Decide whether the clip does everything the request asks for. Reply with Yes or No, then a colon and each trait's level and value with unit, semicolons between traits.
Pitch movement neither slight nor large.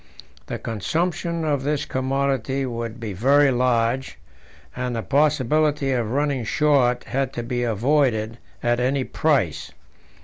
Yes: average, 3.2 semitones